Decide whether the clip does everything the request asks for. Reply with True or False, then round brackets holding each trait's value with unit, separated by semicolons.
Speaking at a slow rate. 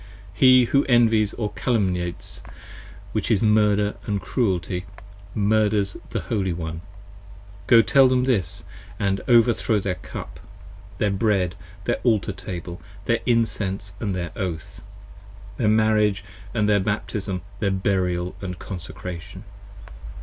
True (120 wpm)